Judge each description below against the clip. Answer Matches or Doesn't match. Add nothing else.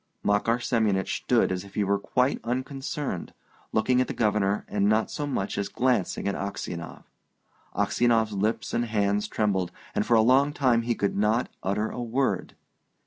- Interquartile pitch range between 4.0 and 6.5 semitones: Doesn't match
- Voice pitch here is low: Matches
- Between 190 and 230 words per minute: Doesn't match